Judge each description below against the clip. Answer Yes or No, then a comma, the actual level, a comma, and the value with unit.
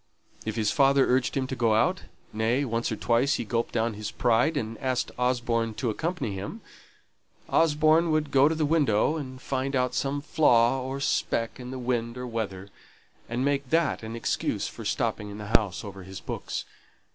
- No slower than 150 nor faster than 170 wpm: No, average, 185 wpm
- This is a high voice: No, low, 125 Hz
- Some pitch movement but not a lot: Yes, average, 3.6 semitones